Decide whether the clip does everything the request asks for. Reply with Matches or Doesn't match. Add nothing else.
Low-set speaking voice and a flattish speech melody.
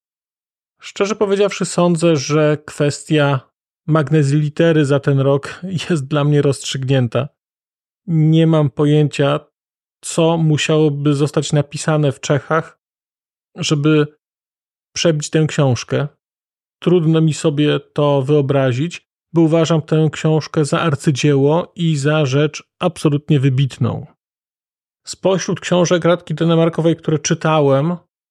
Doesn't match